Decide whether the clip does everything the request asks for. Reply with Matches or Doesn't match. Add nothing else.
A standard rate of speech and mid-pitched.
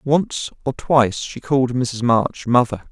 Doesn't match